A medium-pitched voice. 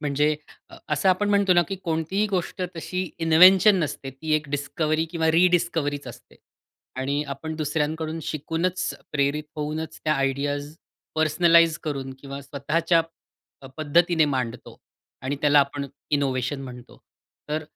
Yes: medium, 155 Hz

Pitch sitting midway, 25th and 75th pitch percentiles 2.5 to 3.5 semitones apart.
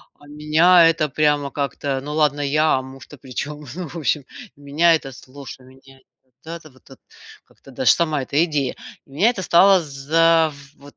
Yes: medium, 150 Hz; average, 2.9 semitones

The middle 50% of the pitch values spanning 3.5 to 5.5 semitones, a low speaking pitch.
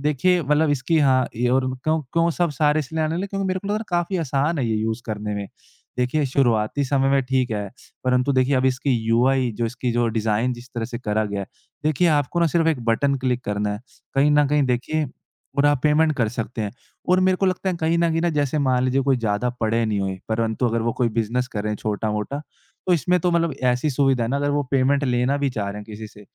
Yes: average, 4.7 semitones; low, 130 Hz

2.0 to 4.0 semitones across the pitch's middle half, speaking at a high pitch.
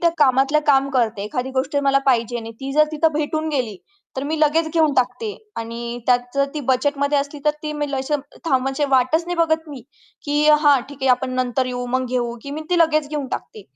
Yes: average, 3.0 semitones; very high, 275 Hz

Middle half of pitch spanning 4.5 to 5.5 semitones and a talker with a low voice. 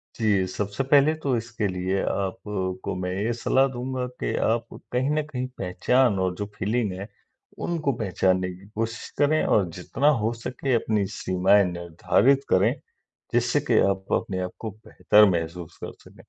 Yes: average, 5.0 semitones; low, 105 Hz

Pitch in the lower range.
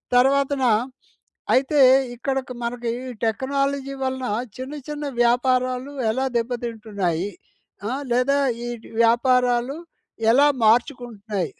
No: very high, 250 Hz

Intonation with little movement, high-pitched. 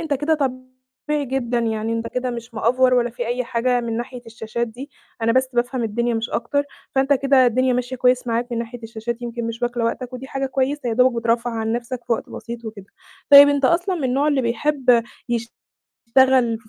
Yes: narrow, 2.1 semitones; high, 245 Hz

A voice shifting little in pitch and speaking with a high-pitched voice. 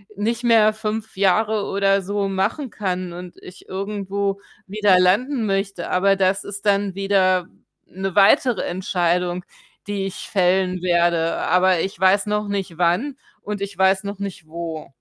Yes: narrow, 2.0 semitones; high, 195 Hz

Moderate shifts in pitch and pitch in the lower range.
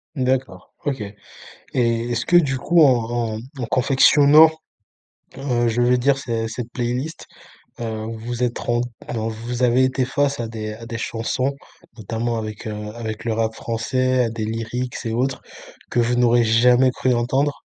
No: narrow, 2.2 semitones; low, 120 Hz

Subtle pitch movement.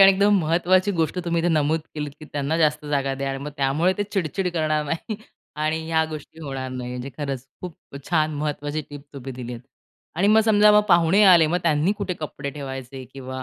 No: average, 4.0 semitones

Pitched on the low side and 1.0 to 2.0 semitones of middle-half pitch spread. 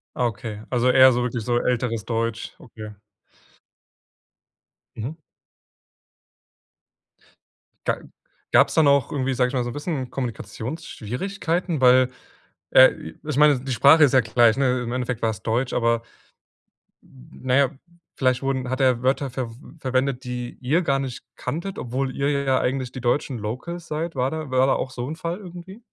No: low, 130 Hz; narrow, 2.5 semitones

